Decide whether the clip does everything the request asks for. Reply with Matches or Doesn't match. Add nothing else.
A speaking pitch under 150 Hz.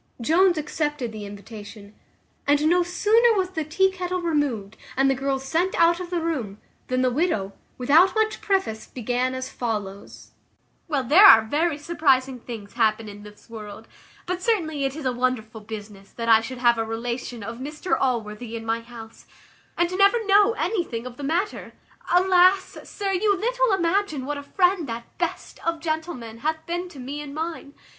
Doesn't match